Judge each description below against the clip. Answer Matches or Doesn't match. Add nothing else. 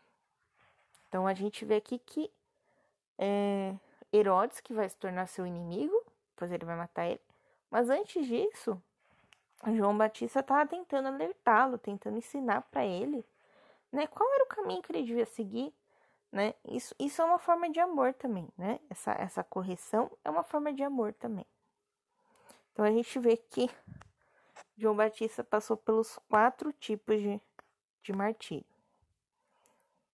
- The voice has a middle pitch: Doesn't match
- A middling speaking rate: Matches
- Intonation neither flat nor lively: Doesn't match